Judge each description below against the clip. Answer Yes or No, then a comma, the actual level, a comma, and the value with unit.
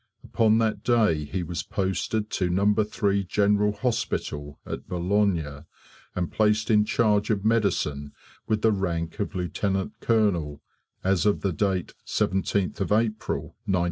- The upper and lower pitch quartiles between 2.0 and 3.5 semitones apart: Yes, average, 3.2 semitones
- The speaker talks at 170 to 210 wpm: No, slow, 135 wpm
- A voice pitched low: Yes, low, 100 Hz